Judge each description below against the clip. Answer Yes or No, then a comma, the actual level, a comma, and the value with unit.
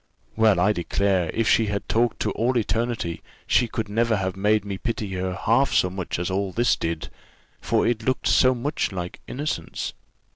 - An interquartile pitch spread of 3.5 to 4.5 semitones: Yes, average, 3.8 semitones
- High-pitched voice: No, low, 105 Hz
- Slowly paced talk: No, average, 185 wpm